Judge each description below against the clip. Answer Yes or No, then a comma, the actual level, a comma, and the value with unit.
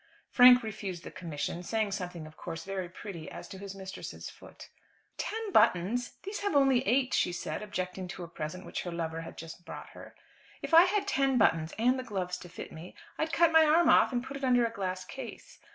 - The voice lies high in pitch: Yes, high, 200 Hz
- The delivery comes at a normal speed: No, fast, 215 wpm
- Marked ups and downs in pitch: Yes, wide, 6.8 semitones